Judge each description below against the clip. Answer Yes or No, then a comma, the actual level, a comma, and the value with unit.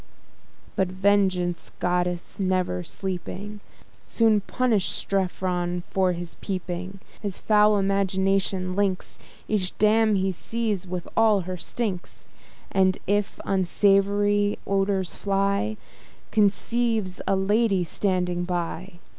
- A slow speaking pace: Yes, slow, 105 wpm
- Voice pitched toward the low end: No, high, 195 Hz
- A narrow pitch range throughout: Yes, narrow, 2.1 semitones